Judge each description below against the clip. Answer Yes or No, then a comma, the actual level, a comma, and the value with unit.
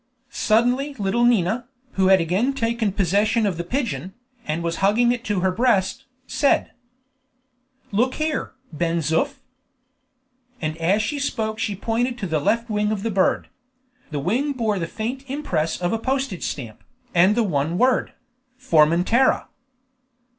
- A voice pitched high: Yes, high, 210 Hz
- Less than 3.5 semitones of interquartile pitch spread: No, wide, 5.5 semitones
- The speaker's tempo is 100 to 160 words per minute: Yes, average, 150 wpm